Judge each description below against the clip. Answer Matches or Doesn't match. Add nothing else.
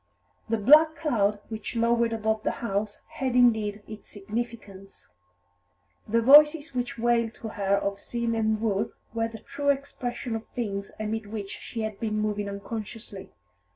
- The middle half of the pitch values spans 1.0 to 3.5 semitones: Matches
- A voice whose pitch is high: Matches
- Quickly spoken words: Doesn't match